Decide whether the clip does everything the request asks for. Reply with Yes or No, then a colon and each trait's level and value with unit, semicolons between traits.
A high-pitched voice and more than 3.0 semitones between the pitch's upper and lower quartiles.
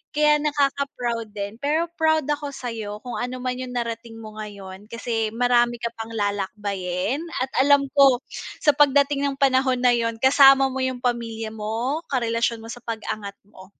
Yes: high, 245 Hz; average, 3.5 semitones